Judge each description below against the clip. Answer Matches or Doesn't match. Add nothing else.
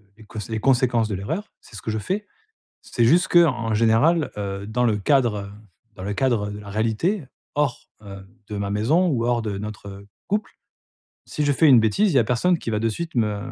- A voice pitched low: Matches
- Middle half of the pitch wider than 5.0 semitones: Matches